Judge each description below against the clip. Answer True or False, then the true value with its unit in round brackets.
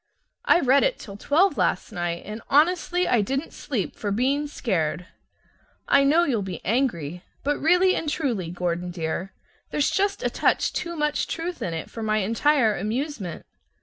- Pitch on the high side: True (245 Hz)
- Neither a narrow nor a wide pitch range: False (8.1 semitones)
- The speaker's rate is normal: True (170 wpm)